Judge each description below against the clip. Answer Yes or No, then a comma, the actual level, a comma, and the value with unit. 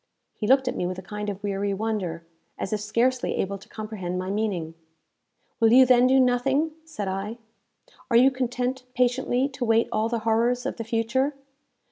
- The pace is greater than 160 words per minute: Yes, average, 185 wpm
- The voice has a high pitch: Yes, high, 230 Hz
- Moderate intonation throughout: Yes, average, 3.7 semitones